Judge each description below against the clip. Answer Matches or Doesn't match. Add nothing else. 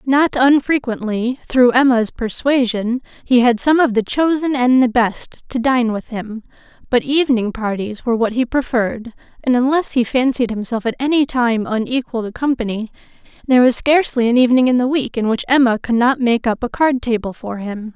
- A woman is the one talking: Matches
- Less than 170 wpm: Doesn't match